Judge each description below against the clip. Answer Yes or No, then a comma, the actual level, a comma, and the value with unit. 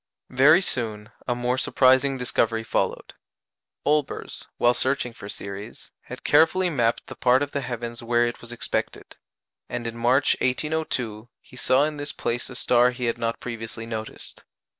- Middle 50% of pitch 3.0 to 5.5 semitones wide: No, narrow, 2.4 semitones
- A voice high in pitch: No, low, 125 Hz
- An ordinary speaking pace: Yes, average, 160 wpm